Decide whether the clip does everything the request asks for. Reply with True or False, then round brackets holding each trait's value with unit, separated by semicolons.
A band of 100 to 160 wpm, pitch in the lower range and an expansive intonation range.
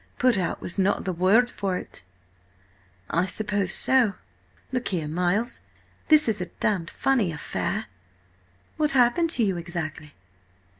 False (140 wpm; 195 Hz; 5.7 semitones)